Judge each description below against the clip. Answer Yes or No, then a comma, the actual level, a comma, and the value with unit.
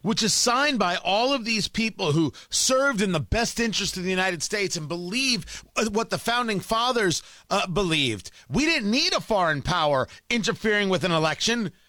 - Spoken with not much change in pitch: No, average, 4.8 semitones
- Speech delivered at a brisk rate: No, average, 180 wpm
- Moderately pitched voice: No, high, 210 Hz